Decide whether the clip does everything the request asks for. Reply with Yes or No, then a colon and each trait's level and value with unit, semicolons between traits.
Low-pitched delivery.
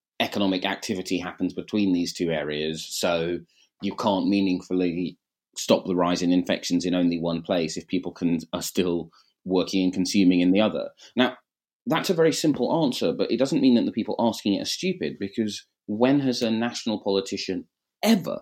Yes: very low, 95 Hz